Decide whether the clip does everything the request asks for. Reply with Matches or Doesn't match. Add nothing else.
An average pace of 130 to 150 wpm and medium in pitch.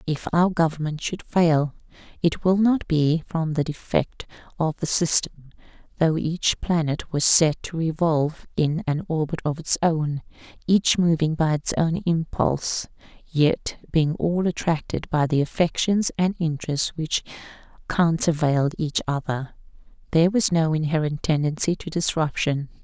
Matches